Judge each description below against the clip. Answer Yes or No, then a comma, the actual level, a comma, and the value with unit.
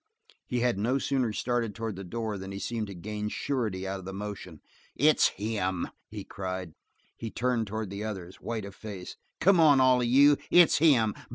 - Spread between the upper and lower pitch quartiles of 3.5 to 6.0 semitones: Yes, average, 4.2 semitones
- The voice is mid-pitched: No, low, 110 Hz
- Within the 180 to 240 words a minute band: Yes, average, 195 wpm